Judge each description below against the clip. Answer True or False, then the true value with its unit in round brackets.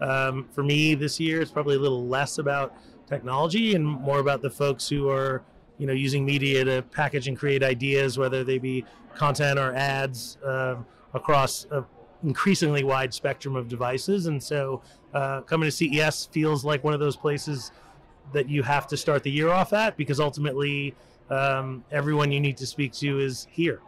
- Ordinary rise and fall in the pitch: False (2.0 semitones)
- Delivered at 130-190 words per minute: True (185 wpm)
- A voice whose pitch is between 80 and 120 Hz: False (140 Hz)